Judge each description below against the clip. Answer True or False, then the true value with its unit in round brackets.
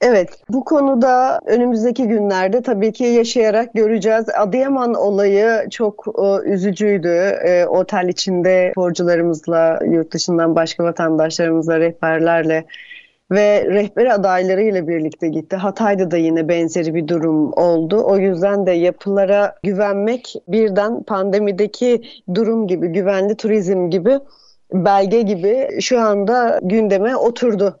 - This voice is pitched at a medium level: False (200 Hz)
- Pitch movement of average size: True (4.1 semitones)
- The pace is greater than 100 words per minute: True (115 wpm)